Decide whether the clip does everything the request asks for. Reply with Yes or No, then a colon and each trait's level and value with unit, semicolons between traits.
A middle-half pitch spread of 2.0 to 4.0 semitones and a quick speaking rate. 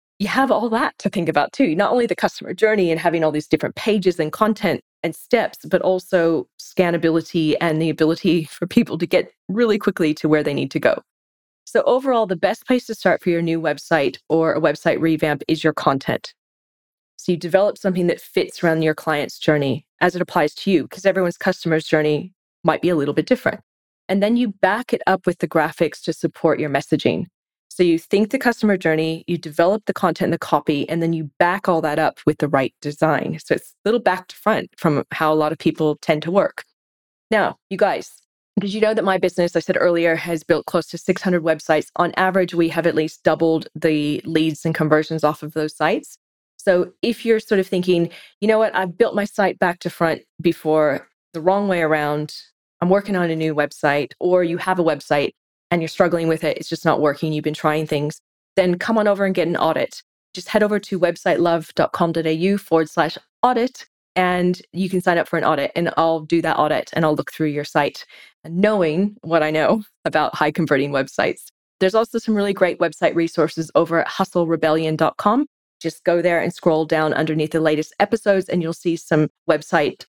Yes: average, 3.2 semitones; fast, 215 wpm